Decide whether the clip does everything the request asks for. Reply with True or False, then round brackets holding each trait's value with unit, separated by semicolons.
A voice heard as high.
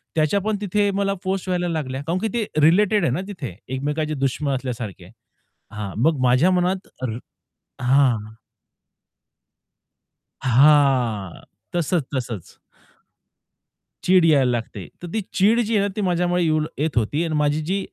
False (155 Hz)